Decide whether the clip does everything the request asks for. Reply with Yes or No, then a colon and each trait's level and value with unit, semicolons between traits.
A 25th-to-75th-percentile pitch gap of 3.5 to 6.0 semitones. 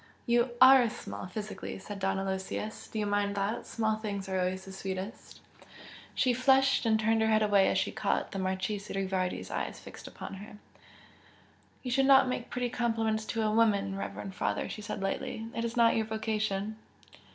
No: average, 2.8 semitones